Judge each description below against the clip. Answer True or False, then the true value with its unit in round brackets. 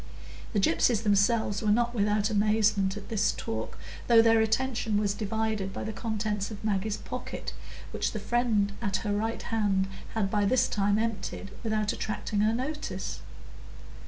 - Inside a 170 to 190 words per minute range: False (160 wpm)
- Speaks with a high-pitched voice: True (215 Hz)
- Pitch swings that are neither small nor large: False (1.8 semitones)